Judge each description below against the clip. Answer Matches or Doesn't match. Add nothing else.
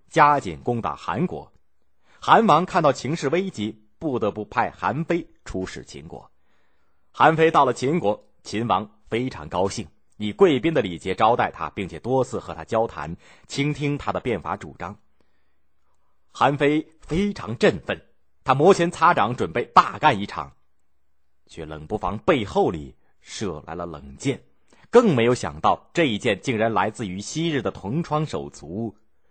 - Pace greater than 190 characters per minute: Matches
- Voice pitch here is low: Matches